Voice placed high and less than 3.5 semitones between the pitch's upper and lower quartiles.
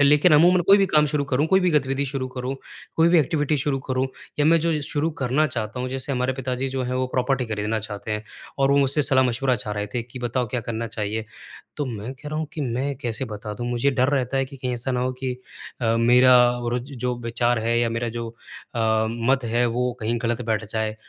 No: low, 125 Hz; average, 3.0 semitones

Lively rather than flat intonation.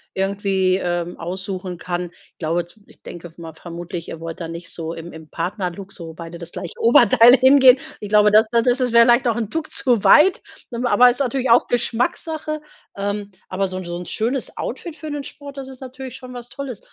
Yes: wide, 6.3 semitones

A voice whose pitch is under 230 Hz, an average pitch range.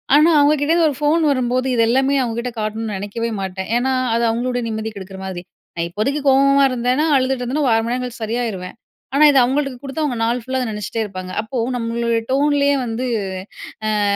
No: high, 245 Hz; average, 3.5 semitones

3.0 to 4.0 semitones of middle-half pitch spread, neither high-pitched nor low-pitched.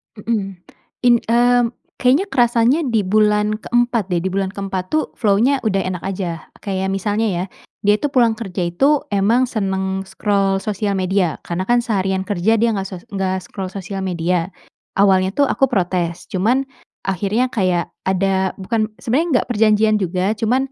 No: average, 3.3 semitones; high, 200 Hz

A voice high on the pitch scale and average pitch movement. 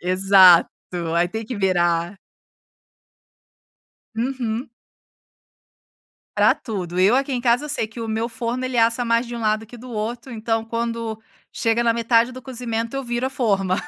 No: high, 230 Hz; narrow, 2.1 semitones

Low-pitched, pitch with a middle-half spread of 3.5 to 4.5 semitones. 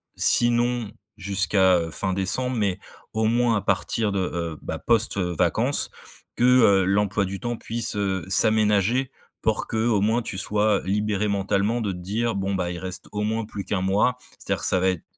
No: low, 105 Hz; average, 2.9 semitones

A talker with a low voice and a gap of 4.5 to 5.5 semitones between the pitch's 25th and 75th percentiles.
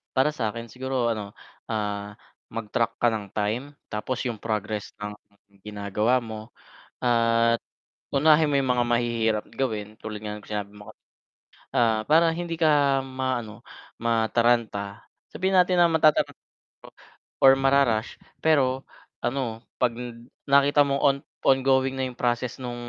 No: low, 120 Hz; average, 3.7 semitones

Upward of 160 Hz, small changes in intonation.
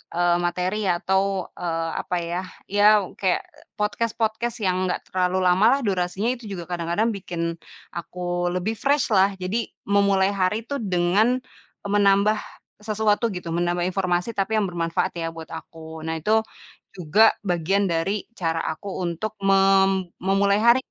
No: high, 190 Hz; average, 3.0 semitones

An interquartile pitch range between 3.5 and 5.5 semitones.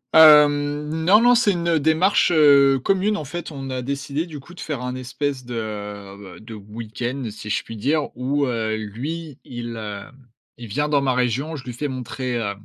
Yes: average, 4.6 semitones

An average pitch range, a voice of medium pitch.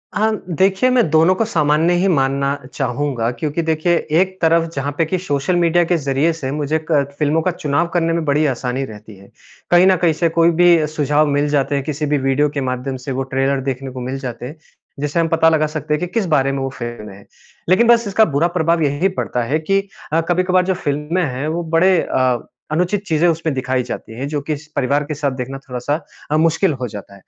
Yes: average, 3.8 semitones; medium, 150 Hz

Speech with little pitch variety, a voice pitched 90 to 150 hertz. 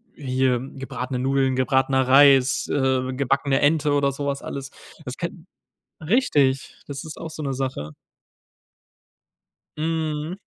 Yes: narrow, 2.2 semitones; low, 135 Hz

